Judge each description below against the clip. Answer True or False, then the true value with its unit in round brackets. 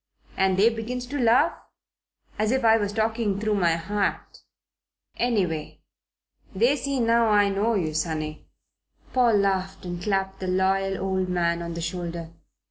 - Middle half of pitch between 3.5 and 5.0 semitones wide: True (4.0 semitones)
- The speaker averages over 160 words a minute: False (150 wpm)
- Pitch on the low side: False (195 Hz)